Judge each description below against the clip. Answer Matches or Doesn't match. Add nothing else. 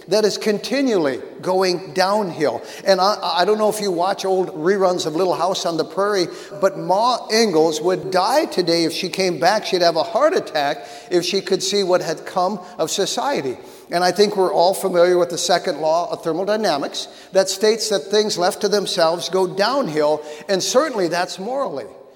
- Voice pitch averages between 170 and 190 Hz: Matches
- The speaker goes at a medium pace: Matches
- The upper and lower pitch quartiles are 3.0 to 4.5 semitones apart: Doesn't match